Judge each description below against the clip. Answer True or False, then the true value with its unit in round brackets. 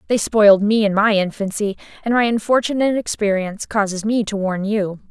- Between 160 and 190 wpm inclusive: True (175 wpm)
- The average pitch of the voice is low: False (210 Hz)